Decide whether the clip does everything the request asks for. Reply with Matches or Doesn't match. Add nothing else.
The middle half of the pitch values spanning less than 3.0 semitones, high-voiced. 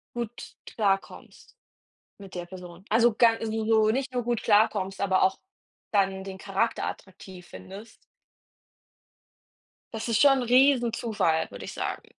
Doesn't match